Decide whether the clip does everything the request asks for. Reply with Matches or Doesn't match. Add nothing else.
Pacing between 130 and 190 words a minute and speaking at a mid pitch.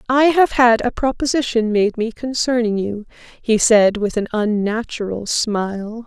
Doesn't match